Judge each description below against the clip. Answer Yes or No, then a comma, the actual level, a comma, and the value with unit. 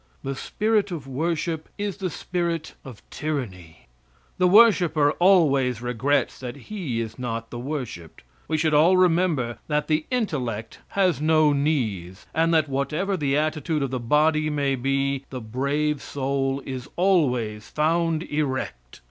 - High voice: No, medium, 145 Hz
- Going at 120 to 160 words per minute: Yes, average, 145 wpm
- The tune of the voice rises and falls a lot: No, average, 4.3 semitones